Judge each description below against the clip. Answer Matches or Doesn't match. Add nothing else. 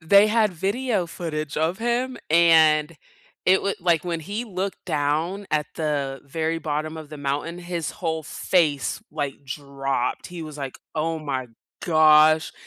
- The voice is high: Doesn't match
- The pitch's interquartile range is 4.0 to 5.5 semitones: Doesn't match